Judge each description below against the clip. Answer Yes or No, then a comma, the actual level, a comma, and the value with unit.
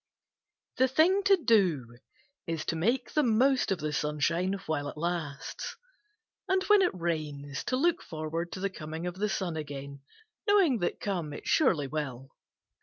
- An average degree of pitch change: No, wide, 8.3 semitones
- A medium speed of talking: Yes, average, 165 wpm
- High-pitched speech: No, medium, 170 Hz